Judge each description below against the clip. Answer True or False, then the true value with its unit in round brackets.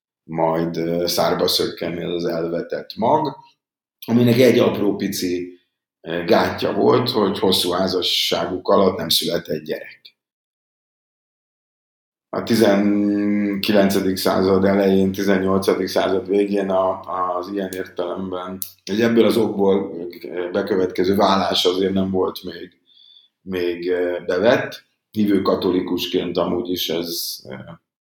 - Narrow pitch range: True (2.1 semitones)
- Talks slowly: True (100 wpm)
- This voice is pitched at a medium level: False (95 Hz)